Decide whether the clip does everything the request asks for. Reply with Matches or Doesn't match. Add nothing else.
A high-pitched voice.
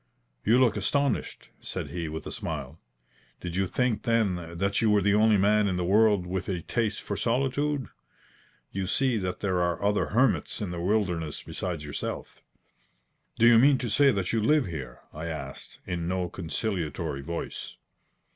Doesn't match